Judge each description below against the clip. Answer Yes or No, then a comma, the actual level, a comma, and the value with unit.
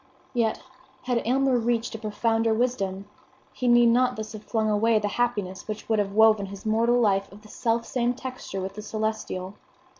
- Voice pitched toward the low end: No, high, 220 Hz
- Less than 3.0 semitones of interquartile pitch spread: Yes, narrow, 2.5 semitones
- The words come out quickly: No, average, 180 wpm